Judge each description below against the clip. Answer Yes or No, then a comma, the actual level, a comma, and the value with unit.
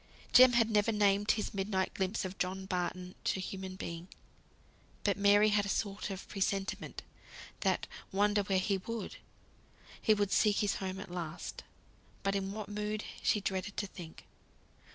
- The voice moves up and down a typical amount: No, narrow, 1.7 semitones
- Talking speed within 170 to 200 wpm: No, average, 160 wpm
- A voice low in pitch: No, high, 200 Hz